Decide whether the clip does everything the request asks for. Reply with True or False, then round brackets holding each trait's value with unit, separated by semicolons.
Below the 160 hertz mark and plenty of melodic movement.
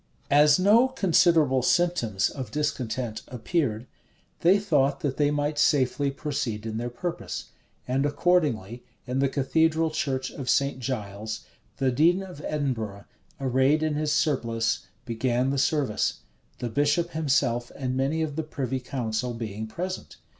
False (135 Hz; 4.2 semitones)